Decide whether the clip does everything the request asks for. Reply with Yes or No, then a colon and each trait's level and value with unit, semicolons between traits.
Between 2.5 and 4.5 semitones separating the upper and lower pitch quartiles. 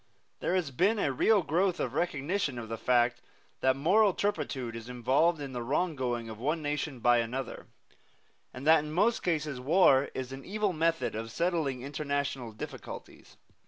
No: average, 5.3 semitones